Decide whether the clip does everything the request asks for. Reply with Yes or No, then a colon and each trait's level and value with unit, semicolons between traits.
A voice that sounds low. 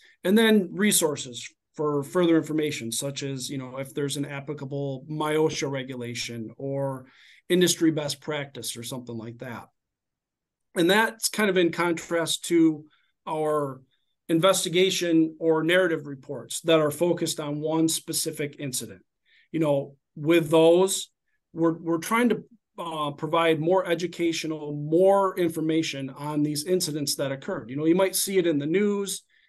No: medium, 160 Hz